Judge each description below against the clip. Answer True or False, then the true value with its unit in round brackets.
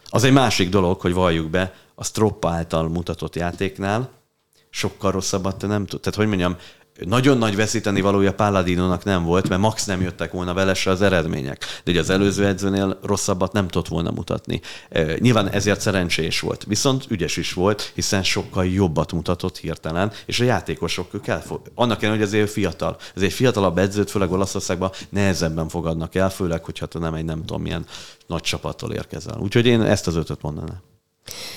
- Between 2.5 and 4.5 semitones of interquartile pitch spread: True (2.9 semitones)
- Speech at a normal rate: False (175 wpm)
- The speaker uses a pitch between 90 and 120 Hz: True (95 Hz)